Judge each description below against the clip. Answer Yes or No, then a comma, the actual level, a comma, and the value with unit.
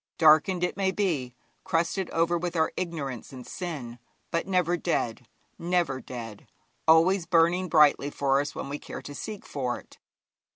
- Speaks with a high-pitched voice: No, medium, 165 Hz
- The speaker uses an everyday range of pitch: Yes, average, 4.4 semitones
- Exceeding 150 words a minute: Yes, average, 160 wpm